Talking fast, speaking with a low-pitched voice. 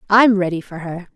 No: fast, 210 wpm; high, 190 Hz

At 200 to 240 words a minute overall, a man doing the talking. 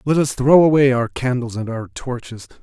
Yes: fast, 205 wpm; male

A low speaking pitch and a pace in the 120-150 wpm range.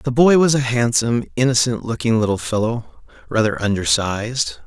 Yes: low, 115 Hz; average, 140 wpm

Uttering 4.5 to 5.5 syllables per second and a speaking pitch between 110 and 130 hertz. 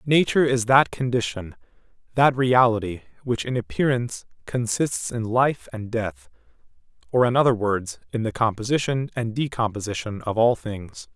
Yes: 4.9 syllables/s; low, 120 Hz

